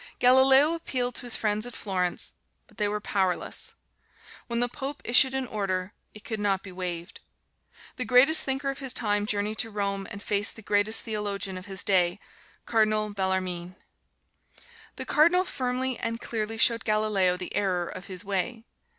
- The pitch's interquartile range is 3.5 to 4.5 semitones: Yes, average, 4.2 semitones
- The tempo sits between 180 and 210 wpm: No, average, 170 wpm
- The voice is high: Yes, high, 210 Hz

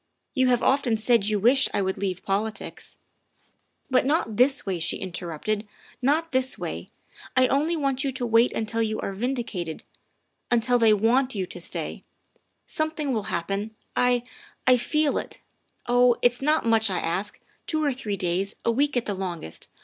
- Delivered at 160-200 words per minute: Yes, average, 185 wpm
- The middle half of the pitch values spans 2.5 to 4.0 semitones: No, average, 4.7 semitones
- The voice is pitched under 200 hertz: No, high, 230 Hz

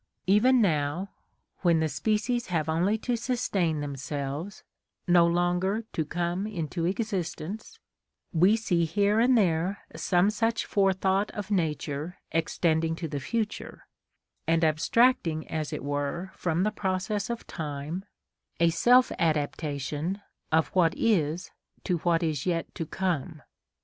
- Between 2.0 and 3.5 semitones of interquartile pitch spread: No, average, 4.3 semitones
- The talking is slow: Yes, slow, 130 wpm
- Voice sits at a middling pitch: Yes, medium, 175 Hz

